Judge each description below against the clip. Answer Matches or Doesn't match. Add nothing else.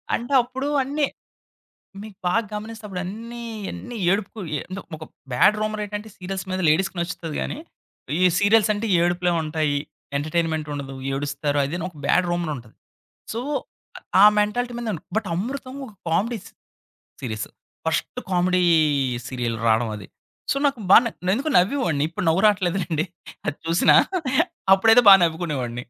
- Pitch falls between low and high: Matches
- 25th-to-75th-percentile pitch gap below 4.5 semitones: Doesn't match